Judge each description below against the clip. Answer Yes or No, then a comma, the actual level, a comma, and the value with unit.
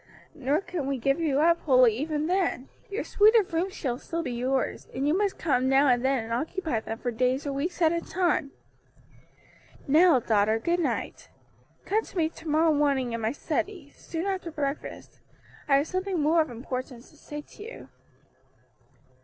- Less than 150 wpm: No, average, 185 wpm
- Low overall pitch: No, very high, 295 Hz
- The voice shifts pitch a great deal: No, average, 4.8 semitones